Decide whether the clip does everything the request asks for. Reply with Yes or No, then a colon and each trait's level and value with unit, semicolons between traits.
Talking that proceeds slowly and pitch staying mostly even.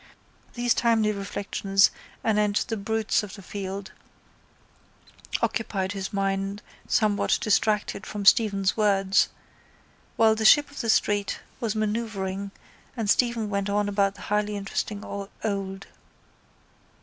Yes: slow, 120 wpm; narrow, 1.8 semitones